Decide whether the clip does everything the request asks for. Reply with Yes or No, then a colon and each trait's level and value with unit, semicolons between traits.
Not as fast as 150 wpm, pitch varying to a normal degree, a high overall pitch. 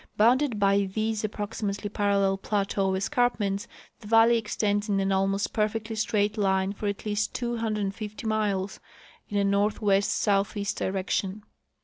No: average, 140 wpm; narrow, 1.6 semitones; high, 205 Hz